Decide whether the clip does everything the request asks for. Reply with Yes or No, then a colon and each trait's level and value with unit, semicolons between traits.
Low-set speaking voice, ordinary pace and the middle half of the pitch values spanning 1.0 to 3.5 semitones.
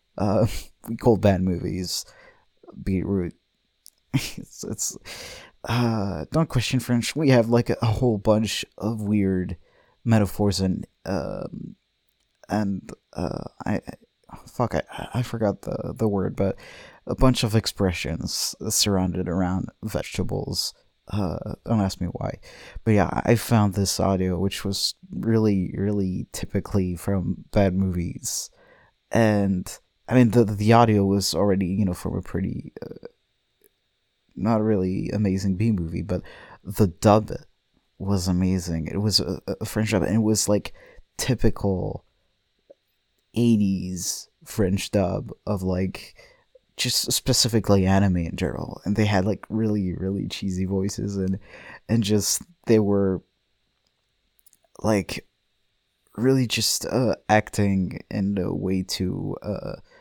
No: low, 100 Hz; slow, 130 wpm; average, 2.9 semitones